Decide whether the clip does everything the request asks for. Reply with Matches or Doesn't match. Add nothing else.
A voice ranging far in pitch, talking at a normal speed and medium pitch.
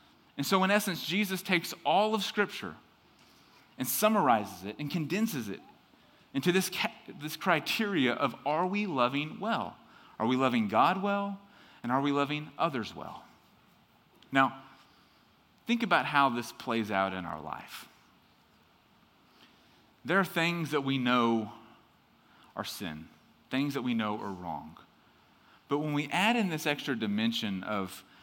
Matches